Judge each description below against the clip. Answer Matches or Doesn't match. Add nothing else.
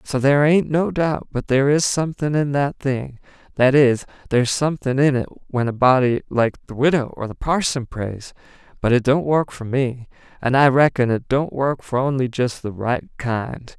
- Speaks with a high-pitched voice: Doesn't match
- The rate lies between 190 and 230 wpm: Matches